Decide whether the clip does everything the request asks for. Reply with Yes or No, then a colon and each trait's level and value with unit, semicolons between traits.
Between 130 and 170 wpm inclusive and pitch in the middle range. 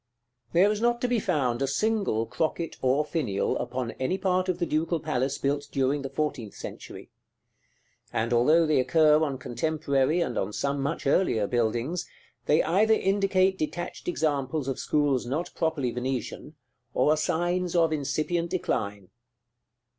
Yes: average, 160 wpm; medium, 150 Hz